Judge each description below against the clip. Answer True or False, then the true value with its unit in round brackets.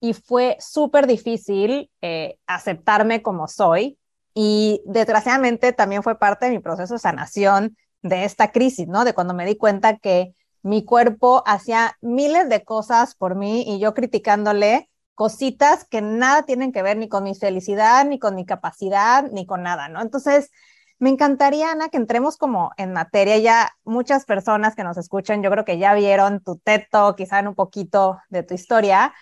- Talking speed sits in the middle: True (175 wpm)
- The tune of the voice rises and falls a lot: False (3.7 semitones)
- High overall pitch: True (215 Hz)